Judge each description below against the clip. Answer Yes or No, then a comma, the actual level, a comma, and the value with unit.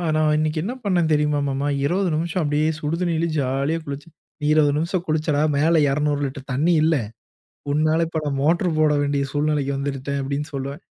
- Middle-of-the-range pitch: Yes, medium, 150 Hz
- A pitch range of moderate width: No, narrow, 2.3 semitones